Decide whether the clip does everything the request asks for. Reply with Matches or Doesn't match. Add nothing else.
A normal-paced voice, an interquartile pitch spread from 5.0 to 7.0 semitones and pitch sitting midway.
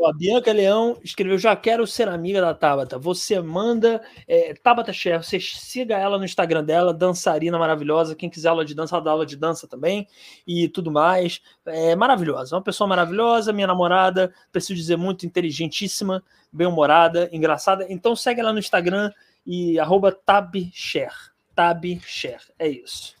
Doesn't match